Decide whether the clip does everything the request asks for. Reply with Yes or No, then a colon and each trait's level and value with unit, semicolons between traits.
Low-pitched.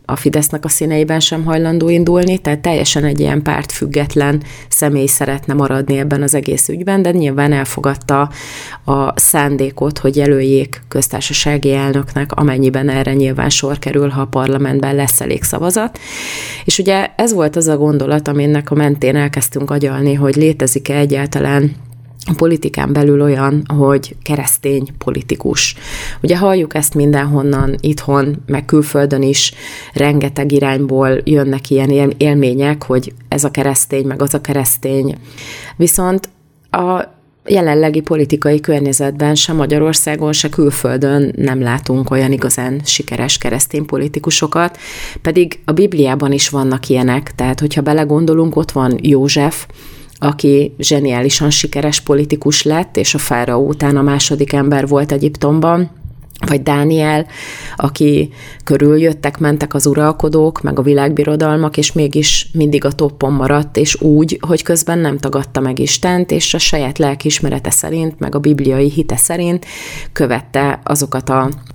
No: medium, 145 Hz